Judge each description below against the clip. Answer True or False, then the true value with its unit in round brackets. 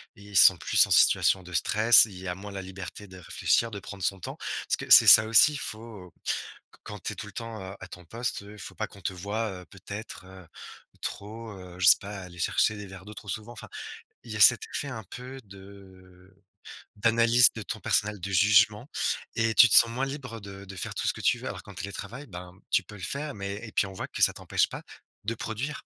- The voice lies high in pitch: False (100 Hz)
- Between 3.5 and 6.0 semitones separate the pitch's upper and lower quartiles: False (3.1 semitones)